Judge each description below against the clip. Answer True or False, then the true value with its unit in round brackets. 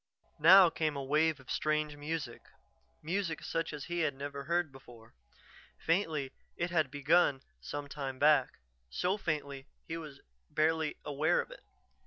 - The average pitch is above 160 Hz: False (150 Hz)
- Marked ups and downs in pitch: False (2.7 semitones)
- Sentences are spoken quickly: False (150 wpm)